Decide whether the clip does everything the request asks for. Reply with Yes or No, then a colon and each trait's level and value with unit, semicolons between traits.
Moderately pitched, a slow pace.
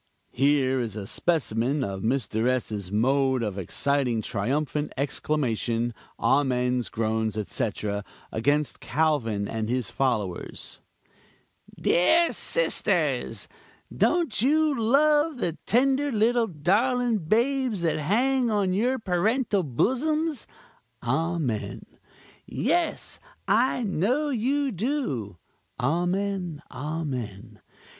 Yes: medium, 155 Hz; slow, 95 wpm